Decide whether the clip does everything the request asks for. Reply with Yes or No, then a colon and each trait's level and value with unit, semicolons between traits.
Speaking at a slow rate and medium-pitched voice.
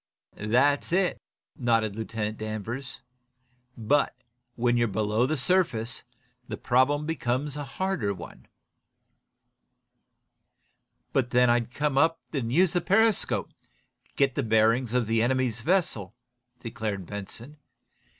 No: slow, 120 wpm; low, 125 Hz